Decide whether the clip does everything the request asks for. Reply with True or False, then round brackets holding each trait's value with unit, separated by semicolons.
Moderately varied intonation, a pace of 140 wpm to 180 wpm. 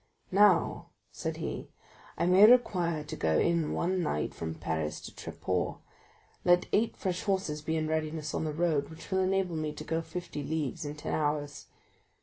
True (3.3 semitones; 175 wpm)